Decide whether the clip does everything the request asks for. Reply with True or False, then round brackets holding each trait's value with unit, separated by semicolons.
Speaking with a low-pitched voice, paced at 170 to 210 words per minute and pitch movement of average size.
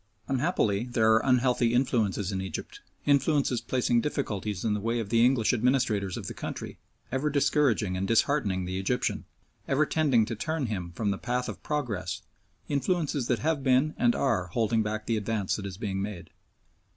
True (115 Hz; 175 wpm; 4.5 semitones)